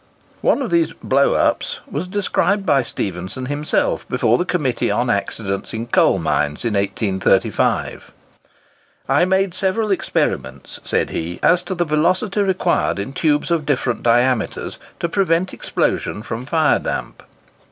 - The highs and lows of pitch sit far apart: Yes, wide, 8.3 semitones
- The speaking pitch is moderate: Yes, medium, 145 Hz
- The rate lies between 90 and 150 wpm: Yes, average, 140 wpm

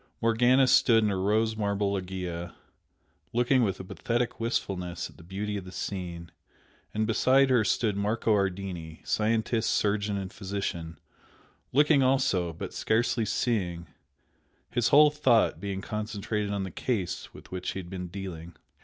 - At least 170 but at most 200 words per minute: No, average, 150 wpm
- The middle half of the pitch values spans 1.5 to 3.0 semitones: No, average, 3.8 semitones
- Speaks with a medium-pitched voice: No, low, 100 Hz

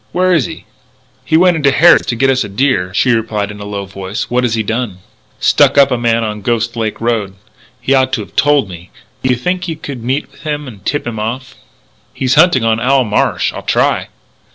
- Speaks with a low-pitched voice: Yes, low, 120 Hz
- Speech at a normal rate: No, fast, 235 wpm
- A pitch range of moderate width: Yes, average, 4.4 semitones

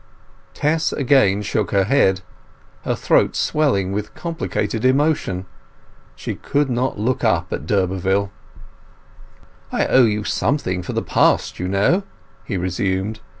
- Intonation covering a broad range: Yes, wide, 6.0 semitones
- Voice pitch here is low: Yes, low, 105 Hz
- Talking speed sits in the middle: No, slow, 130 wpm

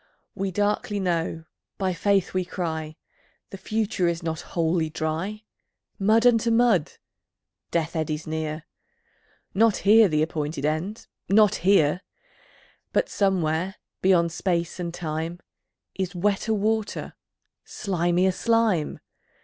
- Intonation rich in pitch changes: No, average, 3.9 semitones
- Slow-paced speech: Yes, slow, 115 wpm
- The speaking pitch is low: No, medium, 180 Hz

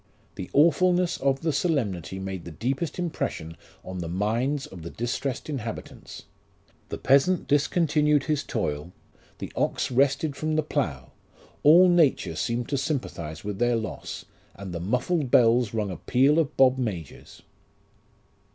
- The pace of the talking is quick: No, average, 150 wpm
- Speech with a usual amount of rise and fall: No, wide, 7.2 semitones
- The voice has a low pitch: Yes, low, 130 Hz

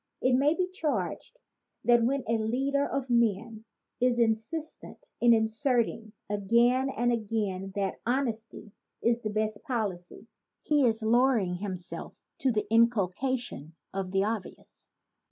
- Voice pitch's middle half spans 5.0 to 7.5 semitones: No, average, 3.3 semitones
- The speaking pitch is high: Yes, high, 230 Hz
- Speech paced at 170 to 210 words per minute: No, slow, 135 wpm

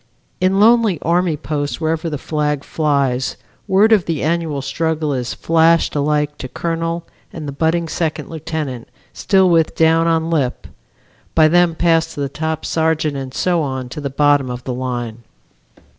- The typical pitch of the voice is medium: Yes, medium, 160 Hz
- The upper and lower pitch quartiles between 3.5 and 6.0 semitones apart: No, average, 2.8 semitones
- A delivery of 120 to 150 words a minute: No, average, 165 wpm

